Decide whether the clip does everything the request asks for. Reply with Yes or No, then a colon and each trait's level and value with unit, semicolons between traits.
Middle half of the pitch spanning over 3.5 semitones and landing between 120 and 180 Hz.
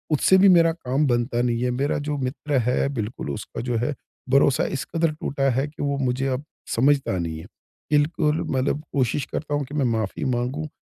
No: average, 3.2 semitones; medium, 140 Hz